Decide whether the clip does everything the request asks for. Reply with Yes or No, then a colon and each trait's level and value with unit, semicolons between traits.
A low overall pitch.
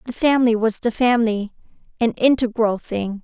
No: high, 230 Hz